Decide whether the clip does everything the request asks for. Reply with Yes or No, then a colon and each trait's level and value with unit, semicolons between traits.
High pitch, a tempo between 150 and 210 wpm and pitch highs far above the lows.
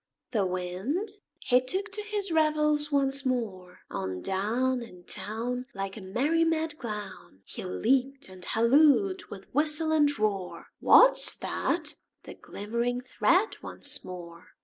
No: very high, 250 Hz; slow, 135 wpm; wide, 7.8 semitones